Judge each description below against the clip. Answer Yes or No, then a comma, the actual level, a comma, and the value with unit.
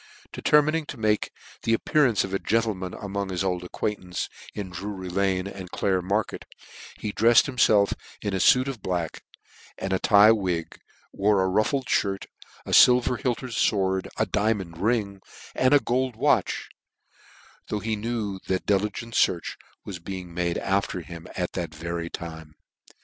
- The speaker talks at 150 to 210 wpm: Yes, average, 155 wpm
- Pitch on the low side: Yes, low, 100 Hz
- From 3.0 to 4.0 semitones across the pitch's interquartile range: Yes, average, 3.5 semitones